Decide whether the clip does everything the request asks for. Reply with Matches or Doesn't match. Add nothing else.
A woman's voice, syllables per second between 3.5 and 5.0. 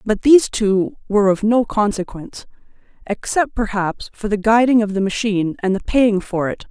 Doesn't match